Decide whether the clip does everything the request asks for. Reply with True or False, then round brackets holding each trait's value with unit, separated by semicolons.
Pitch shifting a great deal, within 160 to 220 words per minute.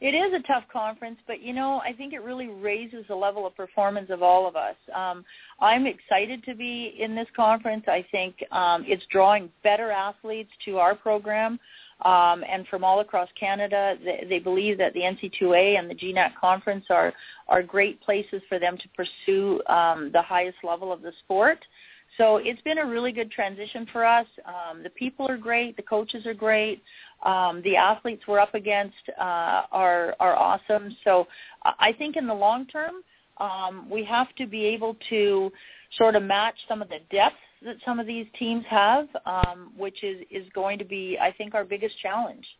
False (3.8 semitones; 195 wpm)